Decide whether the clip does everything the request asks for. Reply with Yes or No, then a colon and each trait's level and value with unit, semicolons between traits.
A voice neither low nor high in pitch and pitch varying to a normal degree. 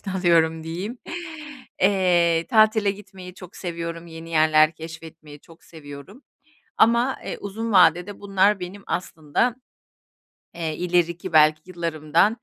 Yes: medium, 175 Hz; average, 3.4 semitones